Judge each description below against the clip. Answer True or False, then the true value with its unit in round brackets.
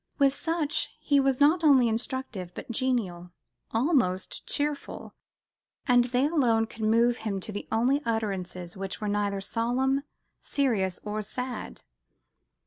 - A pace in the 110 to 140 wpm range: True (135 wpm)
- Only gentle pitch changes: False (4.7 semitones)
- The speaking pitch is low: False (235 Hz)